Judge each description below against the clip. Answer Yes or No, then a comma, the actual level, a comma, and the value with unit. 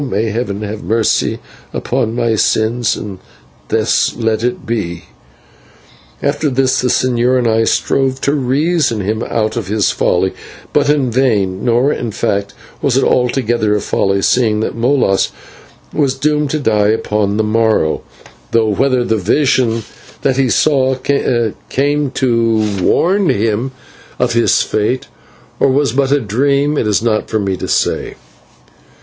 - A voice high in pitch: No, low, 115 Hz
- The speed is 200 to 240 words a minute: No, average, 150 wpm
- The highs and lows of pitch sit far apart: No, average, 3.7 semitones